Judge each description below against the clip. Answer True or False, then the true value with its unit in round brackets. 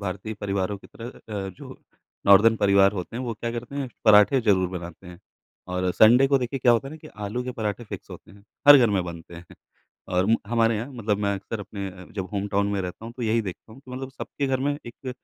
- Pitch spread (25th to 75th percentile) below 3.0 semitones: False (3.7 semitones)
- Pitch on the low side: True (105 Hz)